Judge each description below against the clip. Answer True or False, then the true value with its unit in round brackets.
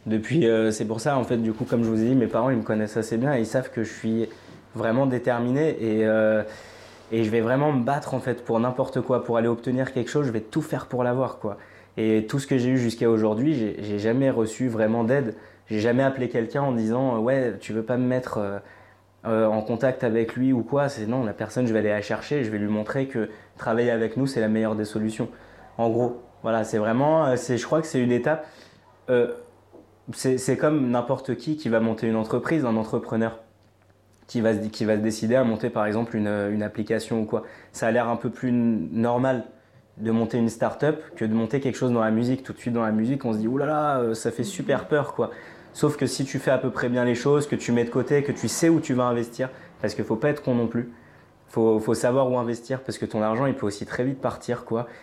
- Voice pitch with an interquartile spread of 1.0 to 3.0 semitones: True (2.7 semitones)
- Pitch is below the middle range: True (120 Hz)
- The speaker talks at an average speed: False (255 wpm)